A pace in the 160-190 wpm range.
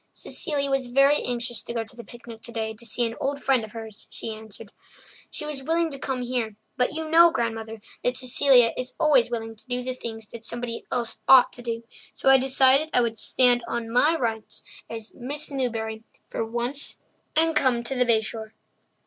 No: average, 200 wpm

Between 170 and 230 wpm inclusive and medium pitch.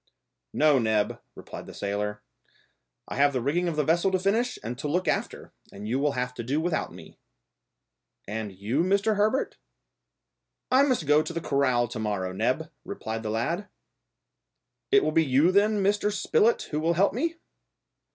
Yes: average, 175 wpm; medium, 150 Hz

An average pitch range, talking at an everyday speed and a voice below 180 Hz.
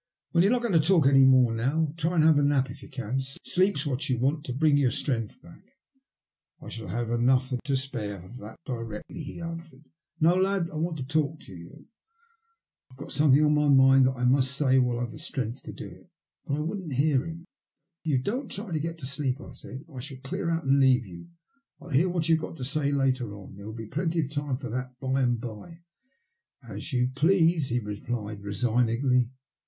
No: average, 4.3 semitones; fast, 235 wpm; low, 135 Hz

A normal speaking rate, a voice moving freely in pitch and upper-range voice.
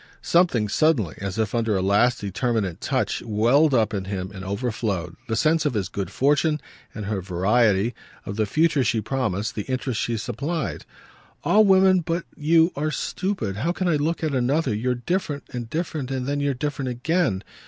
No: average, 185 wpm; wide, 6.7 semitones; low, 125 Hz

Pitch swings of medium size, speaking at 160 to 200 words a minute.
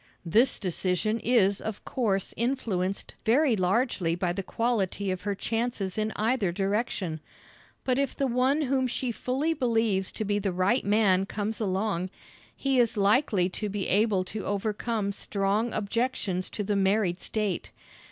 No: average, 3.5 semitones; average, 150 wpm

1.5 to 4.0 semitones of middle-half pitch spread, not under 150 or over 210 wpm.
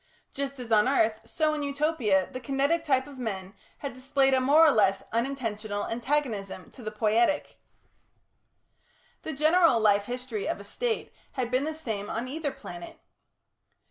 No: average, 4.8 semitones; average, 160 wpm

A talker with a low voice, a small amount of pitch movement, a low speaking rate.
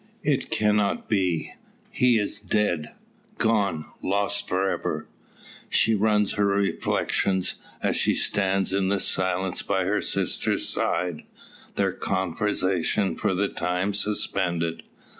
Yes: very low, 95 Hz; narrow, 2.0 semitones; slow, 115 wpm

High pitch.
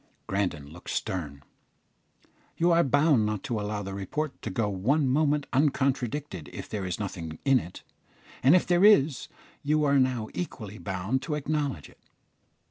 No: low, 125 Hz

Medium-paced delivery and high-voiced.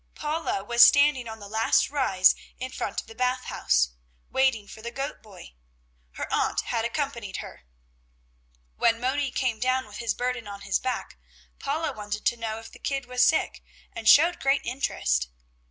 Yes: average, 175 wpm; high, 240 Hz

